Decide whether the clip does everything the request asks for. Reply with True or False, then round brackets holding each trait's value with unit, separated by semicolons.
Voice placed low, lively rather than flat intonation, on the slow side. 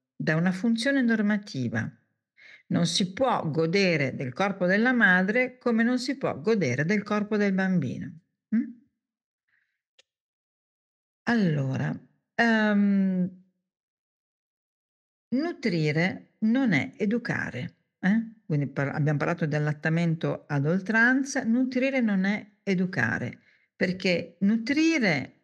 False (195 Hz; 6.2 semitones; 100 wpm)